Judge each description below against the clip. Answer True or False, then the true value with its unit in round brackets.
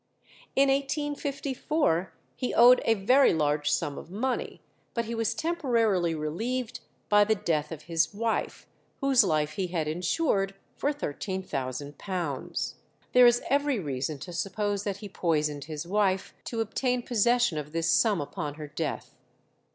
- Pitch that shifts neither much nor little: False (7.8 semitones)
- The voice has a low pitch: False (195 Hz)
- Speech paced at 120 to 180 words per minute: True (145 wpm)